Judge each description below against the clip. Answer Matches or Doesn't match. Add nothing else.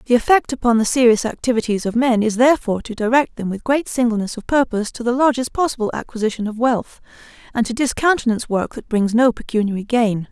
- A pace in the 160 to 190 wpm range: Doesn't match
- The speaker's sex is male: Doesn't match